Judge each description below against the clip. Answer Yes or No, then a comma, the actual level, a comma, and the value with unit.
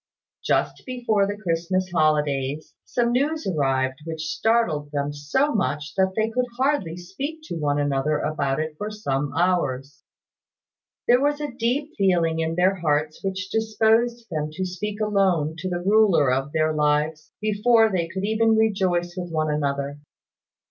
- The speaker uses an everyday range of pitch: No, wide, 6.5 semitones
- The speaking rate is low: No, average, 155 wpm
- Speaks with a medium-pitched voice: Yes, medium, 175 Hz